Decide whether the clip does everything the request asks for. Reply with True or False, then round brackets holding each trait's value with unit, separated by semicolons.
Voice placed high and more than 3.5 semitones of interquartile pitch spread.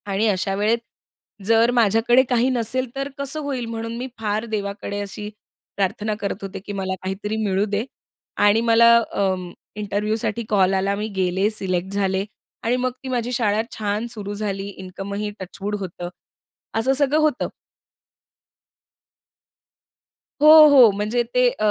False (210 Hz; 2.9 semitones)